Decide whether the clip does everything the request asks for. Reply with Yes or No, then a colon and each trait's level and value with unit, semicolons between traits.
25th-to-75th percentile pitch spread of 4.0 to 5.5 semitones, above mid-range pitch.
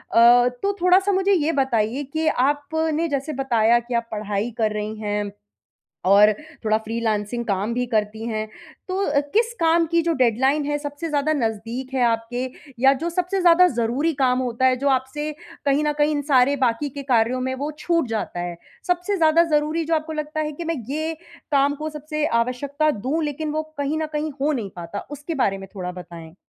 Yes: average, 5.2 semitones; very high, 275 Hz